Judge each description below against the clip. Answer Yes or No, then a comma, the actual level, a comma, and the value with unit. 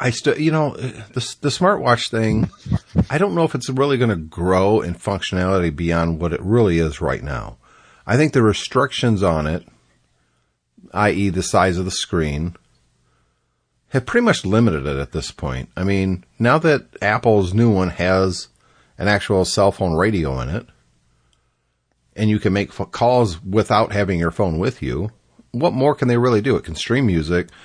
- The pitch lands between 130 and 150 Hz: No, low, 100 Hz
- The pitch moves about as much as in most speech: No, wide, 6.5 semitones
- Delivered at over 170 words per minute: Yes, average, 180 wpm